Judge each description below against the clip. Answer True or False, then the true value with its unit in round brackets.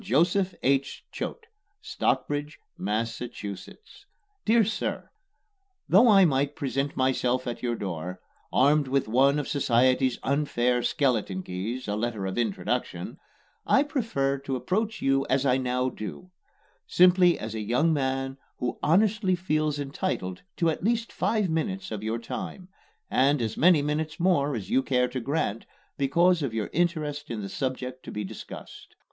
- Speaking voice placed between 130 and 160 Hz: True (135 Hz)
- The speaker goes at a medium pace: True (150 wpm)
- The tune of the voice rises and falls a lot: True (5.8 semitones)